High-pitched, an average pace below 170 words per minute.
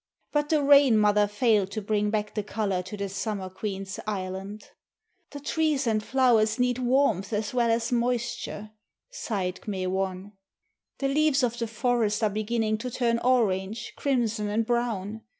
Yes: high, 220 Hz; average, 160 wpm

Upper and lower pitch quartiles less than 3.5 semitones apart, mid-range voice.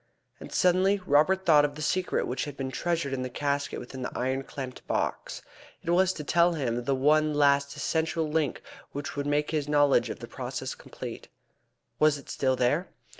Yes: average, 3.0 semitones; medium, 145 Hz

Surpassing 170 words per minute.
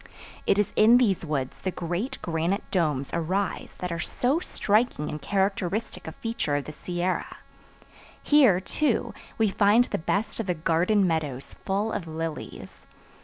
No: average, 155 wpm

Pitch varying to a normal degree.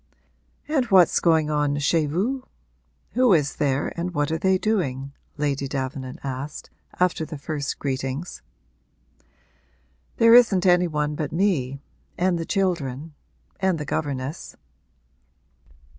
Yes: average, 4.5 semitones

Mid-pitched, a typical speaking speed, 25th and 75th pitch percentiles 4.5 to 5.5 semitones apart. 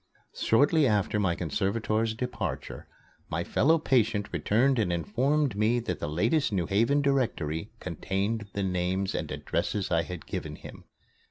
No: low, 105 Hz; average, 145 wpm; average, 5.2 semitones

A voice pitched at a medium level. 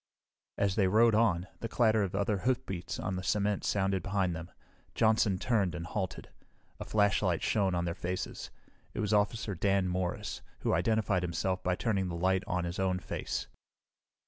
No: very low, 95 Hz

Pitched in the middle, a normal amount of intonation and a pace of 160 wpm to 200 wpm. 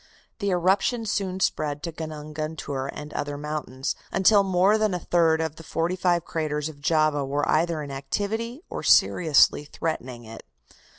Yes: medium, 160 Hz; average, 3.9 semitones; average, 165 wpm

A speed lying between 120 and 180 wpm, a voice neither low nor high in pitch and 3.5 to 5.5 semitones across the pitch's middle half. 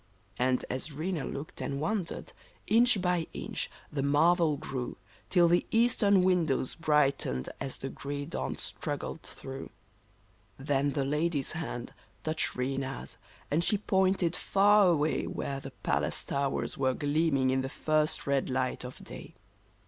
Yes: average, 145 wpm; medium, 150 Hz; average, 4.3 semitones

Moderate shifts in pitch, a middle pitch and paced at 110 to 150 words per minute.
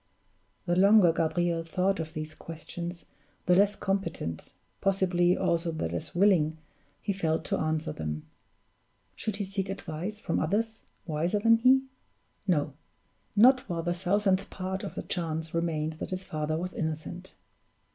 Yes: average, 3.5 semitones; medium, 175 Hz; average, 145 wpm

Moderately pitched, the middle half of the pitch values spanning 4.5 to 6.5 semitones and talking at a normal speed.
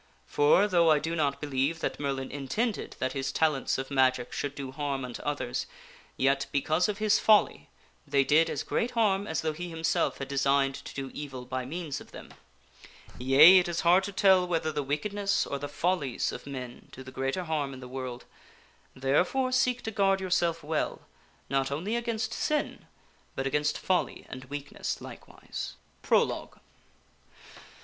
Yes: medium, 145 Hz; average, 5.1 semitones; average, 175 wpm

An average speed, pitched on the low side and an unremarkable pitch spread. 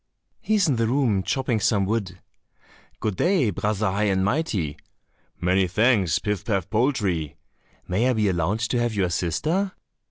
Yes: average, 160 wpm; low, 105 Hz; average, 4.6 semitones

